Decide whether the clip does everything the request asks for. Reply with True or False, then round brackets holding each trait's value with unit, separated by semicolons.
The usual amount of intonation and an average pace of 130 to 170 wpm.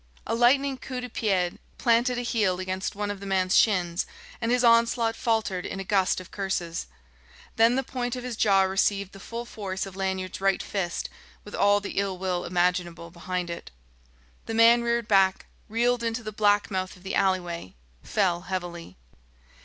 False (3.8 semitones; 180 wpm)